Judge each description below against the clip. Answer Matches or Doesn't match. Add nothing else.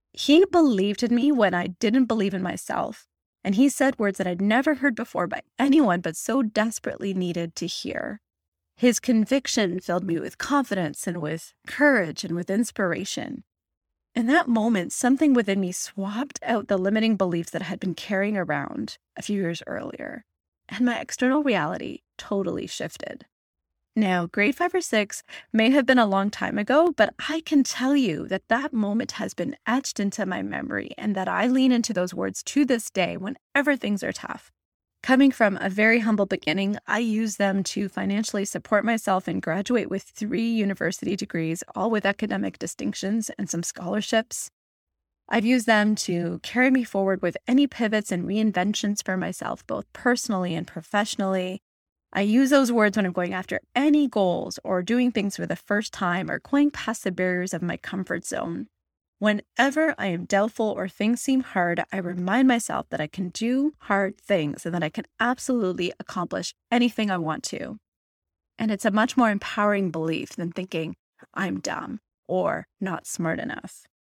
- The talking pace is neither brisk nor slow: Matches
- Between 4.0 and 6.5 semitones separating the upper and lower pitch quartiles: Matches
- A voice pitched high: Matches